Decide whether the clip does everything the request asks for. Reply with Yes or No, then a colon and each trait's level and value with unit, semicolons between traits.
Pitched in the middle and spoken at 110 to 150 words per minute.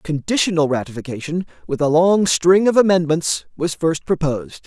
Yes: medium, 160 Hz; average, 140 wpm